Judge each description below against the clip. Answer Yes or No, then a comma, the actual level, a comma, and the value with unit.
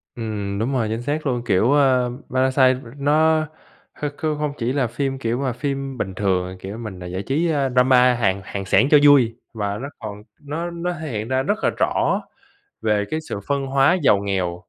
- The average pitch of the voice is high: No, low, 125 Hz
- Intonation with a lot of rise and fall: No, average, 5.0 semitones